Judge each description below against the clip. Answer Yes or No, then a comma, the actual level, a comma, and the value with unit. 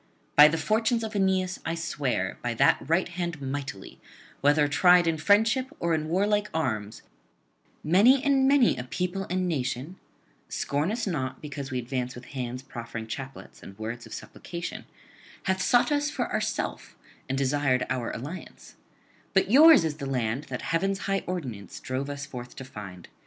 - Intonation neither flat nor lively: No, wide, 6.8 semitones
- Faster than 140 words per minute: Yes, average, 165 wpm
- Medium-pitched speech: Yes, medium, 150 Hz